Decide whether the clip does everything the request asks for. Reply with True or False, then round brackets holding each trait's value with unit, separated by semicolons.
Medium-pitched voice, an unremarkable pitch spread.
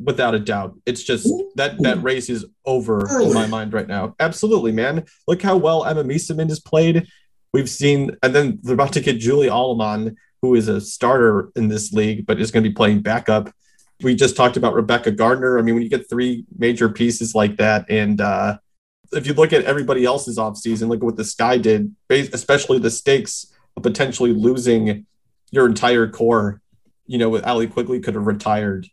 False (120 Hz; 3.9 semitones)